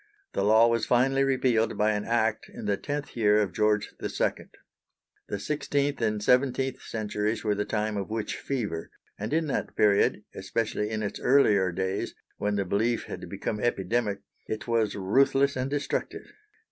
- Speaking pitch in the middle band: No, low, 110 Hz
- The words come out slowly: No, average, 165 wpm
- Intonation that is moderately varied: Yes, average, 3.6 semitones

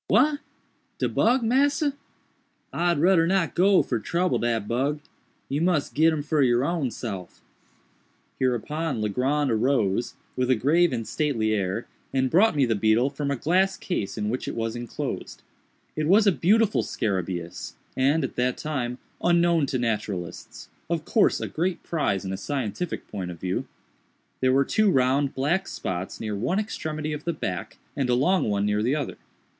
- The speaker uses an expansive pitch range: Yes, wide, 7.0 semitones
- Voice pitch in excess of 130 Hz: Yes, medium, 140 Hz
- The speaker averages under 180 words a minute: Yes, average, 170 wpm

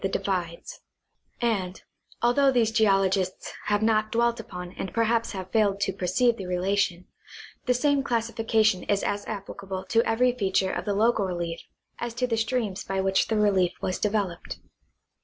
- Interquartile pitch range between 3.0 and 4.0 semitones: Yes, average, 3.3 semitones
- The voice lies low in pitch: No, high, 205 Hz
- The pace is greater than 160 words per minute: Yes, average, 170 wpm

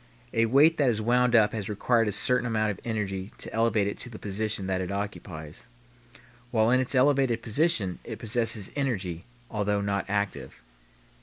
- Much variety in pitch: No, average, 3.2 semitones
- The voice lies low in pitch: Yes, low, 110 Hz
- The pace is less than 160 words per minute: No, average, 175 wpm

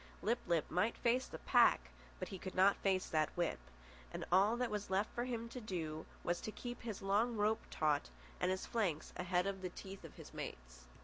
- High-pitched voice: Yes, high, 195 Hz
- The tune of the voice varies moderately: Yes, average, 4.2 semitones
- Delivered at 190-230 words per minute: Yes, fast, 205 wpm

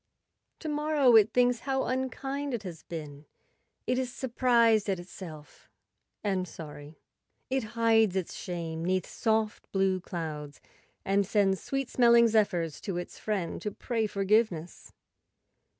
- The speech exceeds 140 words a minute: No, slow, 135 wpm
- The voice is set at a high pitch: Yes, high, 210 Hz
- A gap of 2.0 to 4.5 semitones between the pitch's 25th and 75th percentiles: No, average, 5.3 semitones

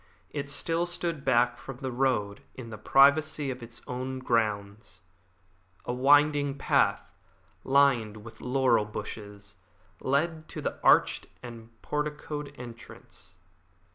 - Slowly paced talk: Yes, slow, 120 wpm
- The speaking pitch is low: Yes, low, 130 Hz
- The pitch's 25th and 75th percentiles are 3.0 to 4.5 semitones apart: Yes, average, 4.1 semitones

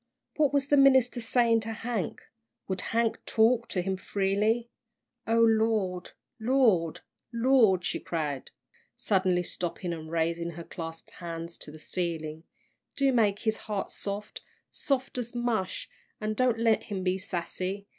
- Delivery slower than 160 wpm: Yes, average, 145 wpm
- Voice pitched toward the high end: Yes, high, 205 Hz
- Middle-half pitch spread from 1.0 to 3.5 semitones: No, average, 4.9 semitones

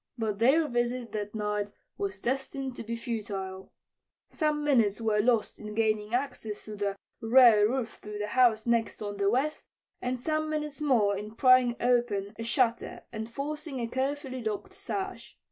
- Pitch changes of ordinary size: Yes, average, 3.8 semitones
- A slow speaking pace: No, average, 165 wpm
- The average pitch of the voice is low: No, high, 235 Hz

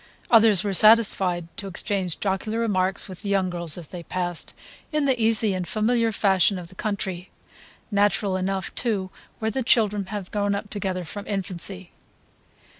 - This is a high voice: Yes, high, 195 Hz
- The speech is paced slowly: No, average, 165 wpm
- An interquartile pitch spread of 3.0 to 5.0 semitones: No, narrow, 2.6 semitones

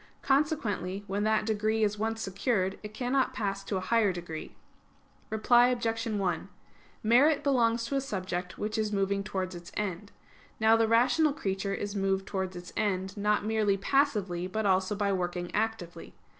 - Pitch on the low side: No, high, 210 Hz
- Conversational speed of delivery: Yes, average, 165 wpm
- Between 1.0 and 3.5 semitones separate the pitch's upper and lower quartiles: Yes, average, 2.9 semitones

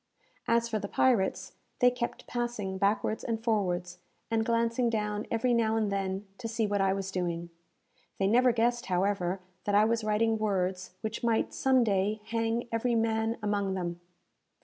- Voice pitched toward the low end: No, high, 215 Hz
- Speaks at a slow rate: No, average, 170 wpm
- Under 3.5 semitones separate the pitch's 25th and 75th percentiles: Yes, average, 3.0 semitones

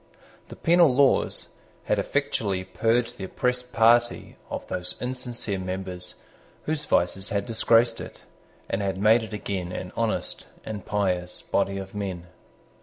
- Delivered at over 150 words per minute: No, average, 140 wpm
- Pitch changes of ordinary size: Yes, average, 4.0 semitones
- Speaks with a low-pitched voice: Yes, low, 105 Hz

